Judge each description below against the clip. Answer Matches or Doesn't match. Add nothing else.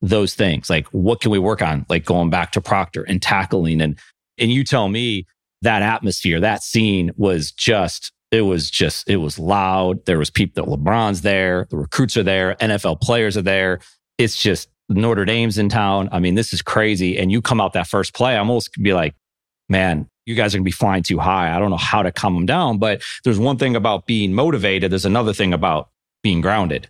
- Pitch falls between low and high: Doesn't match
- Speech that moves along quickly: Matches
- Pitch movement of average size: Matches